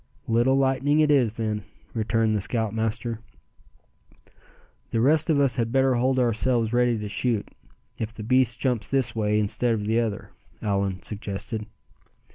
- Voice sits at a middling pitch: No, low, 115 Hz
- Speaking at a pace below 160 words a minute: Yes, average, 150 wpm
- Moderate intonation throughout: Yes, average, 3.0 semitones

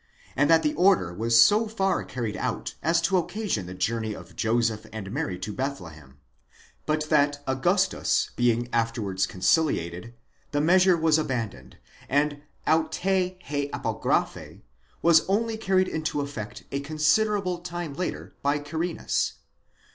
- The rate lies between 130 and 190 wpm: Yes, slow, 135 wpm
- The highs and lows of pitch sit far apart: Yes, wide, 7.2 semitones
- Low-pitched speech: No, medium, 145 Hz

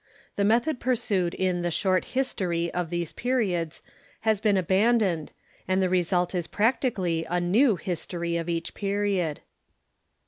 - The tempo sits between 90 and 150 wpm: Yes, average, 140 wpm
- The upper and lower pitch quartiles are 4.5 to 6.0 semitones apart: No, average, 3.6 semitones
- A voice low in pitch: No, medium, 185 Hz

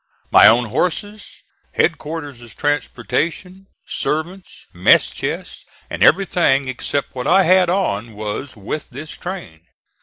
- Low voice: No, medium, 150 Hz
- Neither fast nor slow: No, slow, 115 wpm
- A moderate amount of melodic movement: No, wide, 6.6 semitones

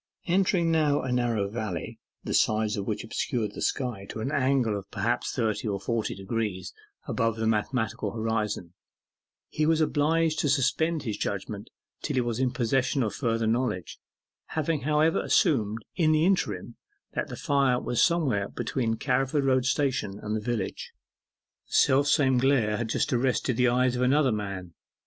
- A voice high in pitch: No, low, 125 Hz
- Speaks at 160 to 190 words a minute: Yes, average, 170 wpm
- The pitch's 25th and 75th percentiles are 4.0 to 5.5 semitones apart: Yes, average, 4.5 semitones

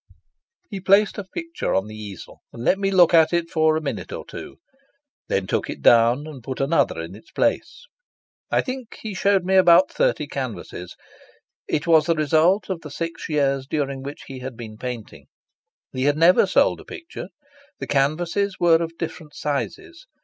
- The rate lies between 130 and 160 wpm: No, average, 185 wpm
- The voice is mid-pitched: Yes, medium, 160 Hz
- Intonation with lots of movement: Yes, wide, 5.7 semitones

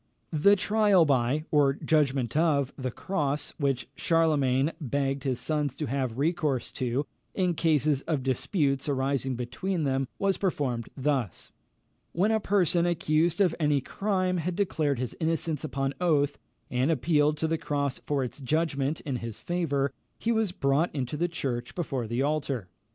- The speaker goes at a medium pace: Yes, average, 155 wpm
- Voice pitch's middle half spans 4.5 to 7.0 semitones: No, average, 3.7 semitones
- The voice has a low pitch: No, medium, 145 Hz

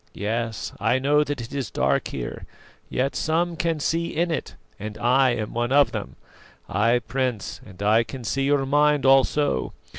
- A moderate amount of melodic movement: Yes, average, 4.3 semitones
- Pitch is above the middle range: No, low, 130 Hz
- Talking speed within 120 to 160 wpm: No, average, 175 wpm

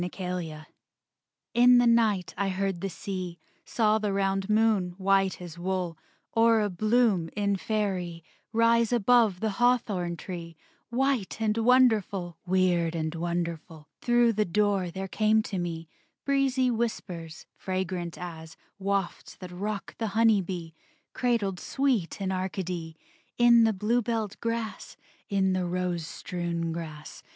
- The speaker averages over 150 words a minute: No, slow, 135 wpm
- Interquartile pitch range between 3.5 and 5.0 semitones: Yes, average, 4.2 semitones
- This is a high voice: Yes, high, 195 Hz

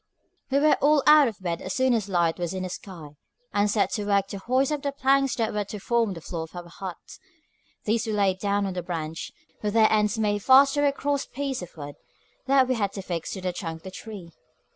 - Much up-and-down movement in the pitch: Yes, wide, 6.1 semitones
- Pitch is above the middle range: Yes, high, 205 Hz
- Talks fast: Yes, fast, 250 wpm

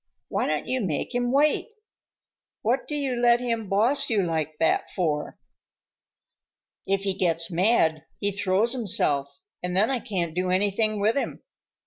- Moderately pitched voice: No, high, 200 Hz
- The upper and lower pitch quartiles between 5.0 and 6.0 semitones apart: Yes, wide, 5.5 semitones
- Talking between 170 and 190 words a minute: No, average, 155 wpm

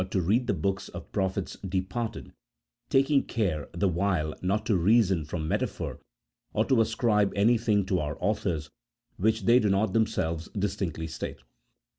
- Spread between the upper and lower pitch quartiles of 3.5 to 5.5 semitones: Yes, average, 4.0 semitones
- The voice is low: Yes, low, 100 Hz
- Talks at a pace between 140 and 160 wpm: Yes, average, 155 wpm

